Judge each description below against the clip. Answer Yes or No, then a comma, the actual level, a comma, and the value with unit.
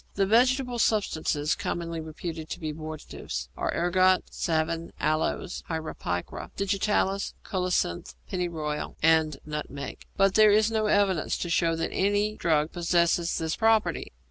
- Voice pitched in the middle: Yes, medium, 170 Hz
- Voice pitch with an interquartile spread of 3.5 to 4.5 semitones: Yes, average, 4.0 semitones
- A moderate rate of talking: No, slow, 130 wpm